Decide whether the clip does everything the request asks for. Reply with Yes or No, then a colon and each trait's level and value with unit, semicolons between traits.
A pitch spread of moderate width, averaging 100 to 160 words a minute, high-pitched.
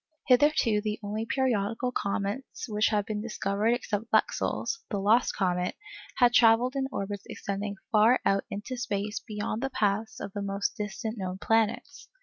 Yes: average, 3.1 semitones; average, 145 wpm; high, 215 Hz